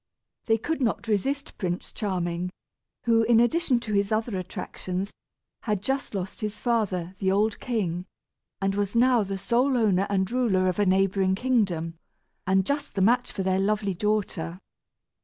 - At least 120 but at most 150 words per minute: No, average, 160 wpm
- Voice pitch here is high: Yes, high, 205 Hz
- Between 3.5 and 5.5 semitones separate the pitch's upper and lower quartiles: Yes, average, 3.8 semitones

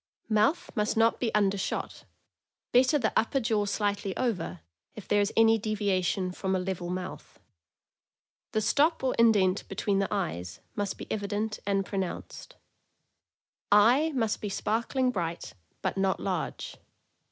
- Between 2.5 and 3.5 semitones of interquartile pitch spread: Yes, average, 2.8 semitones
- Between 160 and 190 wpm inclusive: No, average, 140 wpm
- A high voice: Yes, high, 205 Hz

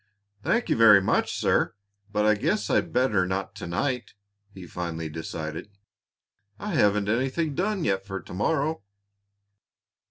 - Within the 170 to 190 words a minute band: No, average, 145 wpm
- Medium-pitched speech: No, low, 105 Hz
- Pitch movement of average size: No, wide, 6.1 semitones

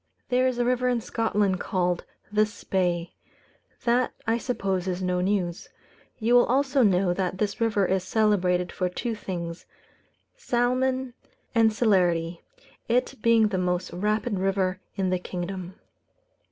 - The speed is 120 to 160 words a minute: Yes, average, 140 wpm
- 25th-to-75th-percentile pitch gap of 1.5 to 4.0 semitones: No, average, 4.6 semitones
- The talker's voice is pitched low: No, high, 200 Hz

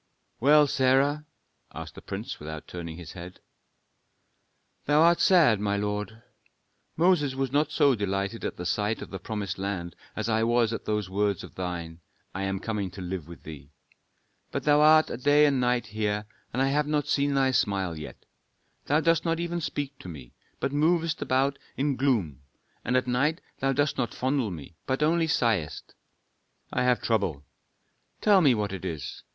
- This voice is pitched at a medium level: No, low, 120 Hz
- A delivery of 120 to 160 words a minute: No, average, 180 wpm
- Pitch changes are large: Yes, wide, 6.9 semitones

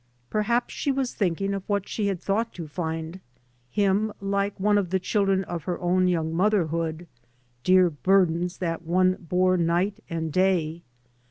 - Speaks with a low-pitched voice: No, medium, 185 Hz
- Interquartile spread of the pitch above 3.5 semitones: No, average, 2.9 semitones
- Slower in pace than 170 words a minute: Yes, average, 160 wpm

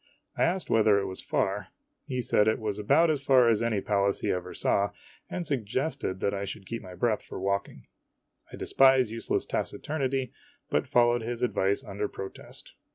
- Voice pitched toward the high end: No, low, 110 Hz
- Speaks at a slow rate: No, average, 185 wpm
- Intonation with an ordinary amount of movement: Yes, average, 4.5 semitones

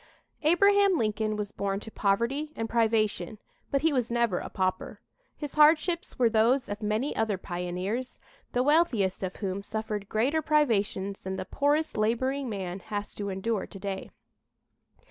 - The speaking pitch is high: Yes, high, 220 Hz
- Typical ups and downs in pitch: No, wide, 5.7 semitones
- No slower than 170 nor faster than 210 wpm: No, average, 155 wpm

